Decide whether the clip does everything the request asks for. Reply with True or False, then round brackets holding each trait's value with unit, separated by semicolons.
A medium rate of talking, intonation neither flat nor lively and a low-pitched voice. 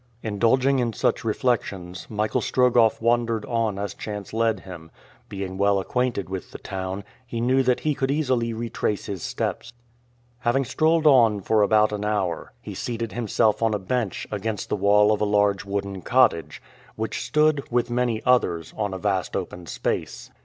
True (170 wpm; 3.4 semitones; 110 Hz)